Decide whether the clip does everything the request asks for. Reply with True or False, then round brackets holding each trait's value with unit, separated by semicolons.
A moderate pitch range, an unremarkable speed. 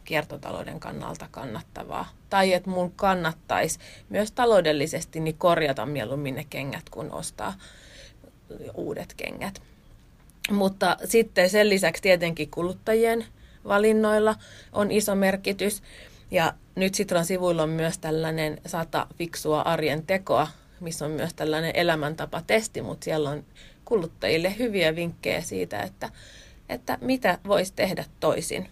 True (4.2 semitones; 120 wpm)